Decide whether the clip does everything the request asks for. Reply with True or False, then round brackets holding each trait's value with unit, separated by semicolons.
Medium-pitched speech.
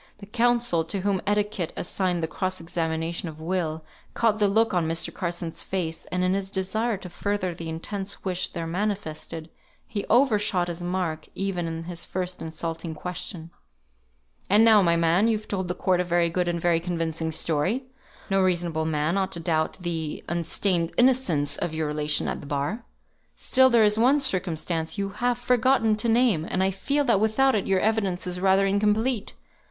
True (180 Hz)